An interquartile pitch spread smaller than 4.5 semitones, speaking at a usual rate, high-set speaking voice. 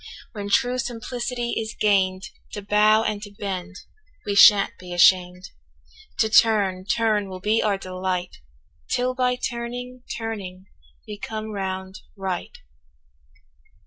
No: average, 3.2 semitones; slow, 125 wpm; high, 205 Hz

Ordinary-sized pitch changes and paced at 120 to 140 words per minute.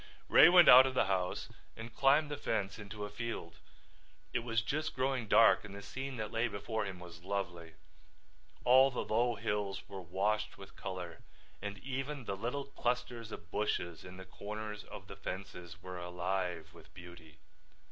No: average, 4.7 semitones; average, 175 wpm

